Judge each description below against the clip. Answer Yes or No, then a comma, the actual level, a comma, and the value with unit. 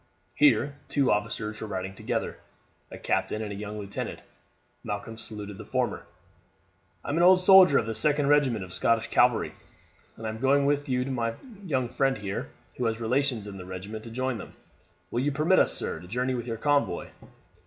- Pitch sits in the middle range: No, low, 115 Hz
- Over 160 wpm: Yes, average, 185 wpm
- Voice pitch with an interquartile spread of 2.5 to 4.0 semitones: No, average, 4.8 semitones